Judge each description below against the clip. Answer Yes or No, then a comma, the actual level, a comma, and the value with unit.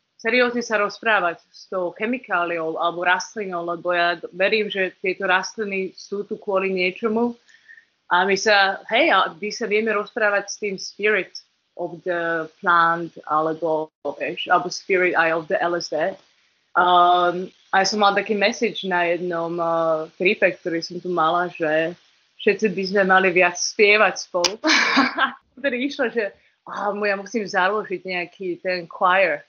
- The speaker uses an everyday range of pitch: Yes, average, 3.3 semitones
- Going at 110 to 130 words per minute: No, average, 150 wpm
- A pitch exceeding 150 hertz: Yes, medium, 185 Hz